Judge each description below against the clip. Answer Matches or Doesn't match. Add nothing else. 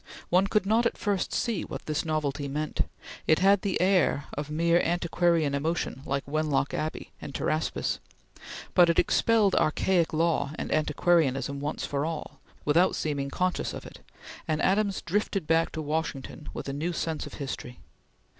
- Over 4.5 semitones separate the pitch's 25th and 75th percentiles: Doesn't match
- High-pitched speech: Doesn't match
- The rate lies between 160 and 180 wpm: Matches